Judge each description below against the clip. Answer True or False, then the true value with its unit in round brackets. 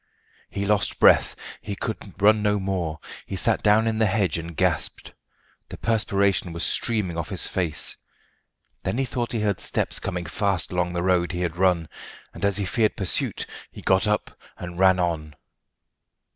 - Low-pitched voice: True (95 Hz)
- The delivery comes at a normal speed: True (175 wpm)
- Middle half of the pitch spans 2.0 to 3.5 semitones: True (3.1 semitones)